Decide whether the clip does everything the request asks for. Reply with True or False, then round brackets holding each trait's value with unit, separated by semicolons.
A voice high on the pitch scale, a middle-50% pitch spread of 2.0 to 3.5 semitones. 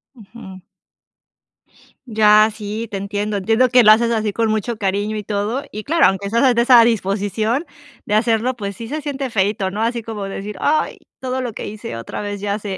True (215 Hz; 2.6 semitones)